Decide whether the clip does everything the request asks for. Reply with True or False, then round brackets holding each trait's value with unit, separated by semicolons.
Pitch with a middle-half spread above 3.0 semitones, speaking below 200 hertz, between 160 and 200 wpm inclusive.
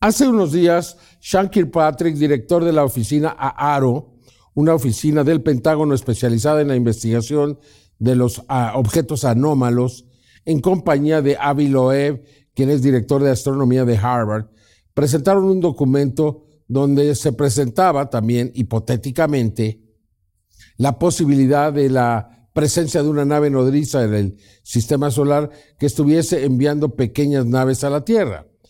False (3.6 semitones; 140 Hz; 135 wpm)